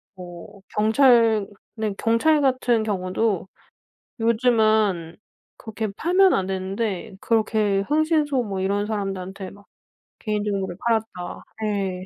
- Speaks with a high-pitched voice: Yes, high, 215 Hz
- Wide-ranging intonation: No, average, 3.0 semitones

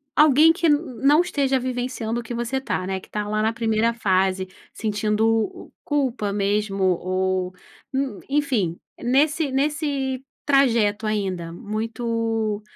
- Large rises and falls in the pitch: No, average, 4.7 semitones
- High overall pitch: Yes, high, 230 Hz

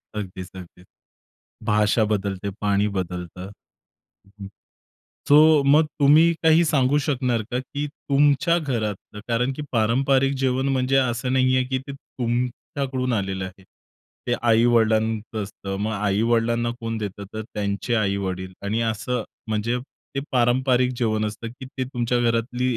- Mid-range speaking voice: No, low, 120 Hz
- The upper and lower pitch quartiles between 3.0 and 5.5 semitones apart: Yes, average, 3.7 semitones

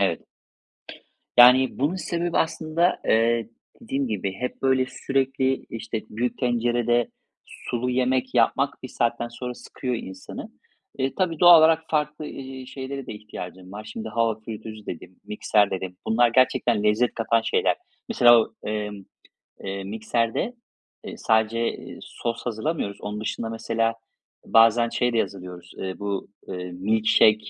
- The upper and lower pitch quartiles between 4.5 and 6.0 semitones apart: No, average, 3.5 semitones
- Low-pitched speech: Yes, low, 115 Hz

